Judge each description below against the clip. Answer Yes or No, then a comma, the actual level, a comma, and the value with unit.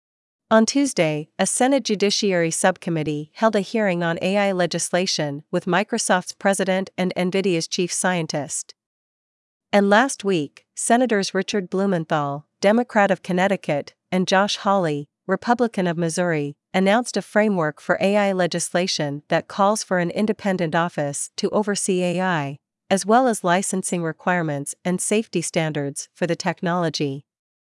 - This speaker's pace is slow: Yes, slow, 130 wpm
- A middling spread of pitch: Yes, average, 3.3 semitones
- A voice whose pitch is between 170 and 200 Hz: Yes, medium, 185 Hz